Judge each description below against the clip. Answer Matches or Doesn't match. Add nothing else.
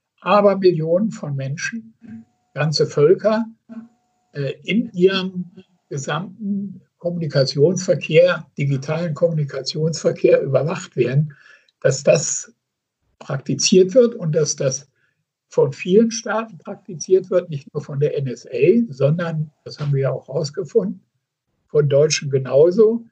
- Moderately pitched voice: Matches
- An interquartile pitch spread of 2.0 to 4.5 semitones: Doesn't match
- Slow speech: Matches